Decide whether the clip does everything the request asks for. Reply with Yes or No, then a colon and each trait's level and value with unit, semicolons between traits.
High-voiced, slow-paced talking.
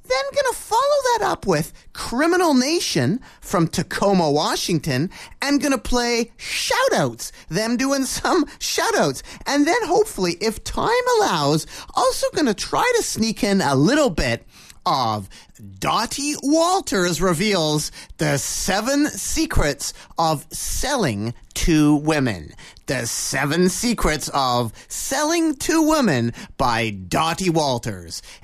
Yes: high, 200 Hz; slow, 120 wpm